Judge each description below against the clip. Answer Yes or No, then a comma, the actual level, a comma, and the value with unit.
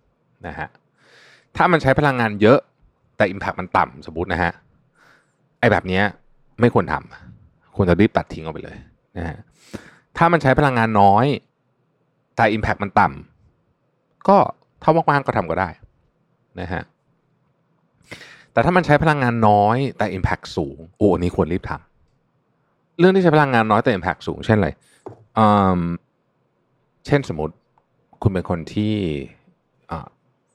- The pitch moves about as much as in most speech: No, wide, 6.5 semitones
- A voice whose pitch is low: Yes, low, 110 Hz